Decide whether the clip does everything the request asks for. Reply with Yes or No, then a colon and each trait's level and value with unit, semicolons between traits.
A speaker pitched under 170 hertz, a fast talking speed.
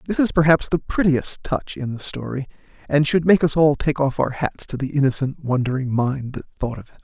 Yes: medium, 140 Hz; fast, 230 wpm